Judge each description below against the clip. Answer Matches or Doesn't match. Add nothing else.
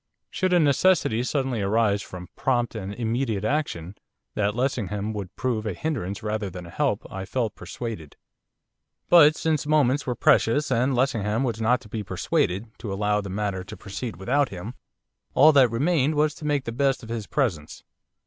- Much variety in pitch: Doesn't match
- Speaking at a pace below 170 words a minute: Doesn't match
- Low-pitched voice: Matches